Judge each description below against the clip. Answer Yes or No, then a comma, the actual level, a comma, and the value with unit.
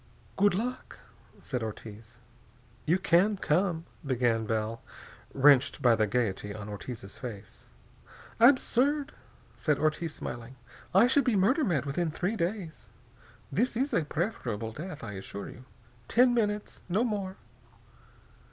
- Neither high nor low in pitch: Yes, medium, 160 Hz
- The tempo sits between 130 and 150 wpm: Yes, slow, 135 wpm